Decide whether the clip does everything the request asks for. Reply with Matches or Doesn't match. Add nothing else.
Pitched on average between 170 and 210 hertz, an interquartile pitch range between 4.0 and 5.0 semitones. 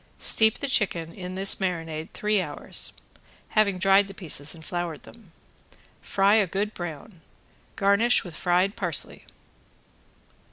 Doesn't match